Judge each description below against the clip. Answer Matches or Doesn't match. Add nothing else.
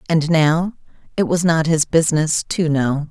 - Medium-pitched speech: Matches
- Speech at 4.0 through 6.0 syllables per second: Matches